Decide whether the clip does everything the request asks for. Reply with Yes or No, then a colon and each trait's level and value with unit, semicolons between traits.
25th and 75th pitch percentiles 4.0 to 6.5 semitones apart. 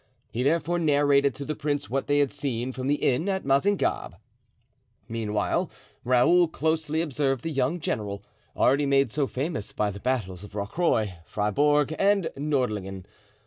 Yes: average, 4.8 semitones